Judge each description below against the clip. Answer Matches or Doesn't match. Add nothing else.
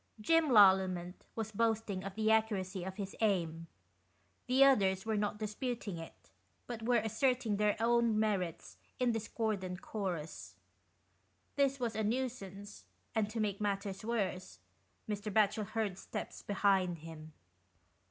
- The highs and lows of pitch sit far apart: Doesn't match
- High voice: Matches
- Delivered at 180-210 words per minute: Doesn't match